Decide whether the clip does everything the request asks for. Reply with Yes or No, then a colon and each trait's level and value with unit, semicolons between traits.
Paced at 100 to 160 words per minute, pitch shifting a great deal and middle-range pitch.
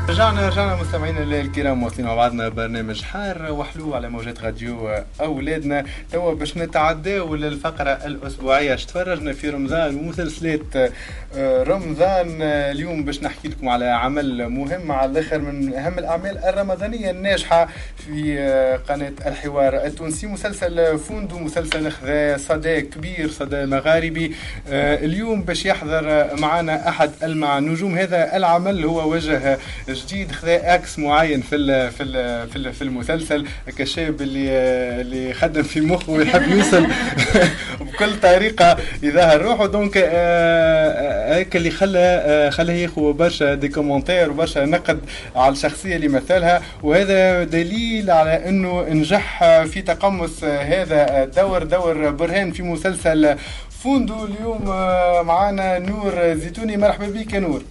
No: average, 130 wpm; average, 4.2 semitones; medium, 160 Hz